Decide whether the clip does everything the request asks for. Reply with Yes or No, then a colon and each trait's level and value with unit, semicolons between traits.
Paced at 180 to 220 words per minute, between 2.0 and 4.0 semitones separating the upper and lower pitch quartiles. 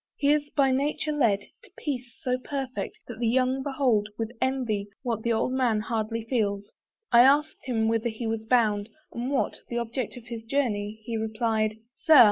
Yes: average, 185 wpm; average, 3.0 semitones